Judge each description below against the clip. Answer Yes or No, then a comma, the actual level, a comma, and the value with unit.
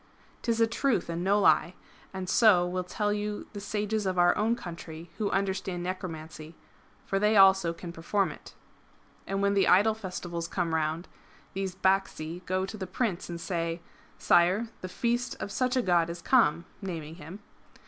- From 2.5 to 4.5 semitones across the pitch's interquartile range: Yes, average, 3.3 semitones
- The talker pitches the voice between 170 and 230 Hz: Yes, medium, 185 Hz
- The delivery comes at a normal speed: Yes, average, 180 wpm